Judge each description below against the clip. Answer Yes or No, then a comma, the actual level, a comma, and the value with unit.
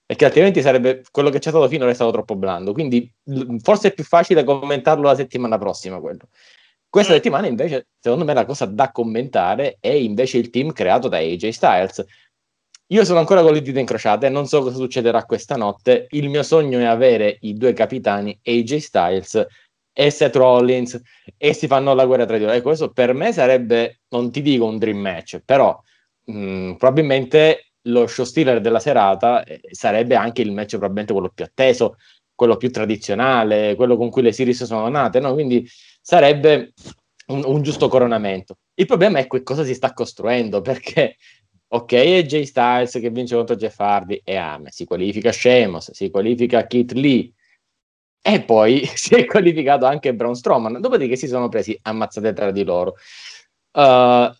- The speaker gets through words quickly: Yes, fast, 180 wpm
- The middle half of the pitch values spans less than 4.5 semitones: Yes, average, 3.6 semitones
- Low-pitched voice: Yes, low, 125 Hz